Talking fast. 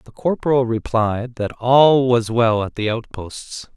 No: average, 160 wpm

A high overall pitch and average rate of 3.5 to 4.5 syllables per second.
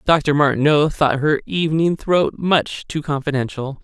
No: medium, 150 Hz; 4.4 syllables/s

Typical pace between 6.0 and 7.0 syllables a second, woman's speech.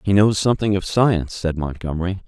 No: 6.1 syllables/s; male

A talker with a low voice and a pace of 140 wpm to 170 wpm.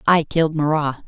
No: medium, 155 Hz; average, 165 wpm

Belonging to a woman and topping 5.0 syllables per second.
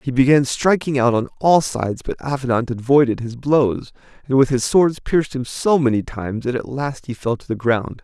No: male; 5.2 syllables/s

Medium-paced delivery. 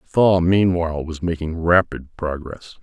Yes: average, 150 wpm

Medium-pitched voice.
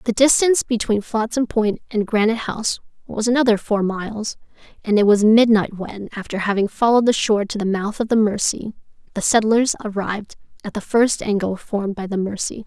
No: high, 215 Hz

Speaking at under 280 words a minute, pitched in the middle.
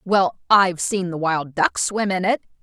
Yes: fast, 205 wpm; medium, 175 Hz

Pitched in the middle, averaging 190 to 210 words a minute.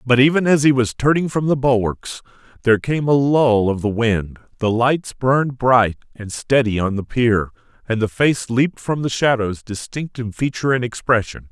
No: low, 125 Hz; average, 195 wpm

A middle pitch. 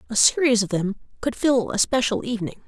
No: high, 230 Hz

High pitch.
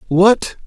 Yes: high, 195 Hz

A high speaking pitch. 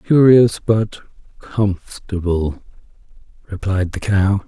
No: low, 100 Hz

